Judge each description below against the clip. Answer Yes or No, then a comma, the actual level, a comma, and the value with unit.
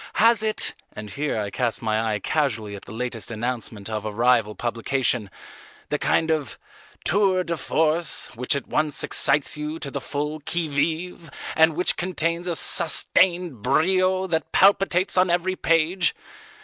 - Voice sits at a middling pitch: Yes, medium, 155 Hz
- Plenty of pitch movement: Yes, wide, 6.5 semitones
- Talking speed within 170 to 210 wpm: No, average, 160 wpm